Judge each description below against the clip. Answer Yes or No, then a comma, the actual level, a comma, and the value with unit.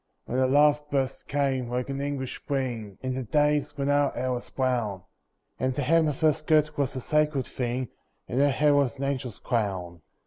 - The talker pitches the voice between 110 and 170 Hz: Yes, low, 135 Hz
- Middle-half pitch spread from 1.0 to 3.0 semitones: Yes, narrow, 2.5 semitones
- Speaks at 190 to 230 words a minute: Yes, average, 200 wpm